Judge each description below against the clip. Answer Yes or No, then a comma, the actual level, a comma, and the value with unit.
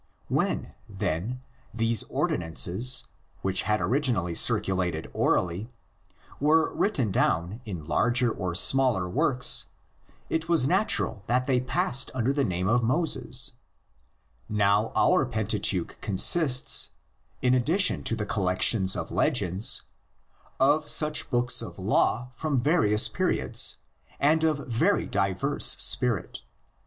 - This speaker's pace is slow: Yes, slow, 120 wpm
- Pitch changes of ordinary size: No, wide, 6.0 semitones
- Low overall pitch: Yes, low, 120 Hz